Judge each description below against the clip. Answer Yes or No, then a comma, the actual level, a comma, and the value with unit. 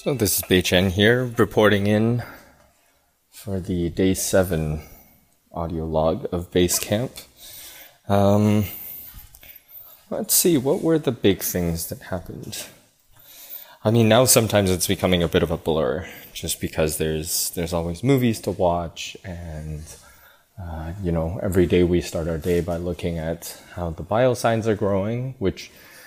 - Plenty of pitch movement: No, average, 3.6 semitones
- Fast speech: No, average, 150 wpm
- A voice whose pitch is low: Yes, very low, 90 Hz